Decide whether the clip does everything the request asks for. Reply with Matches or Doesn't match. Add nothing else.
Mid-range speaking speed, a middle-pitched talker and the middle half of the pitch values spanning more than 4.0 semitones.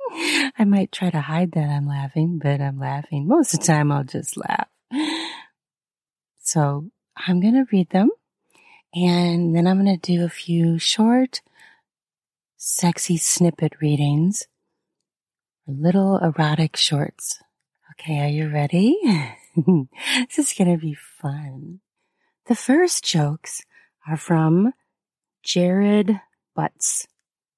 Doesn't match